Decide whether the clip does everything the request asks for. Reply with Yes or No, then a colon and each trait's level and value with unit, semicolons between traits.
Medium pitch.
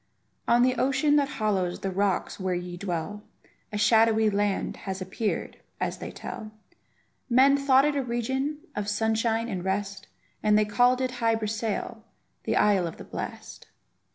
No: high, 220 Hz